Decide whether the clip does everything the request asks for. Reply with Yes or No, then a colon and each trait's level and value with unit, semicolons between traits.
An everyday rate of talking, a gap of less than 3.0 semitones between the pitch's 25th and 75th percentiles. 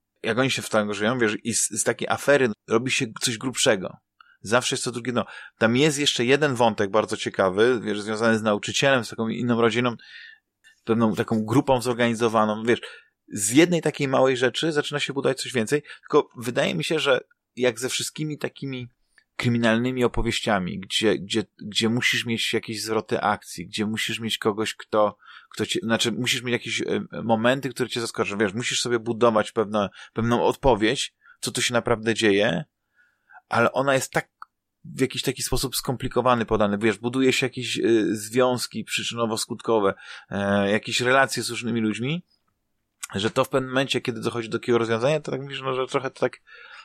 No: fast, 175 wpm; narrow, 2.5 semitones